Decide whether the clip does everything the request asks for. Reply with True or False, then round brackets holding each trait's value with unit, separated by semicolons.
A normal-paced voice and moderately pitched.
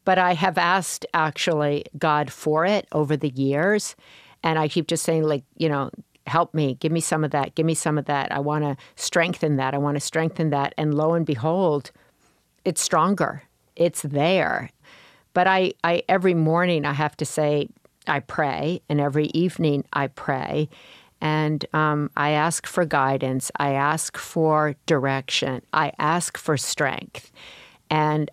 True (170 wpm; 155 Hz)